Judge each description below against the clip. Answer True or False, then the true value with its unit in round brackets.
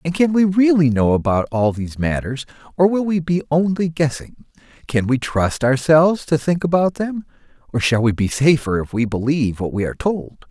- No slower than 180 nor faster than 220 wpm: True (200 wpm)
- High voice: False (145 Hz)